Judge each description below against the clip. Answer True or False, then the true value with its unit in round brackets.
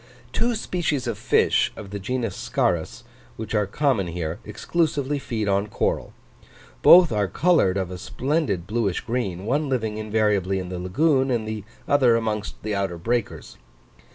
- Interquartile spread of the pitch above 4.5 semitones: True (5.4 semitones)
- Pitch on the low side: True (110 Hz)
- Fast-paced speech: False (155 wpm)